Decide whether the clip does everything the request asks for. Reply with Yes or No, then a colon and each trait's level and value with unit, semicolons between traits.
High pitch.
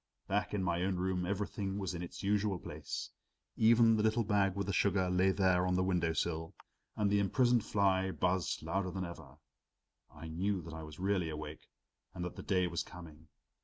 No: very low, 95 Hz